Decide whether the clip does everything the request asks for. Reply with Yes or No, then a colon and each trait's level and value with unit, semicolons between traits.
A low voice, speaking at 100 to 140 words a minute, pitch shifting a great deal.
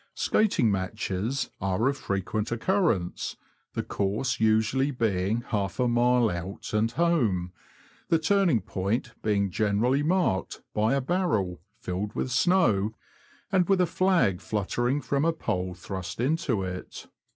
Yes: low, 115 Hz; slow, 135 wpm; wide, 6.4 semitones